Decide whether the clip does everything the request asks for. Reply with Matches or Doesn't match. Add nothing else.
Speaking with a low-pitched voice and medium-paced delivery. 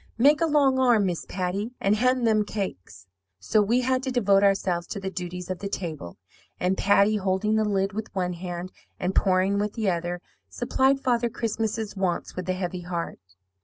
Doesn't match